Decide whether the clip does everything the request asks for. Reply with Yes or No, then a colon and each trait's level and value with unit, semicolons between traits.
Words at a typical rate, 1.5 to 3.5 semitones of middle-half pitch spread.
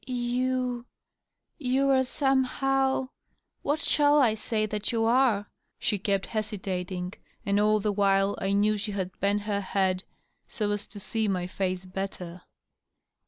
No: average, 145 wpm; average, 4.3 semitones